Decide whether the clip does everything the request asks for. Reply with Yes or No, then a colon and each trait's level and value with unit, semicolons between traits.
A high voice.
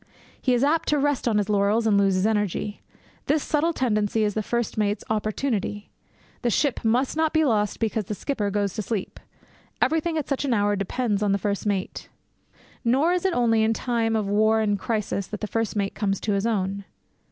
Yes: high, 220 Hz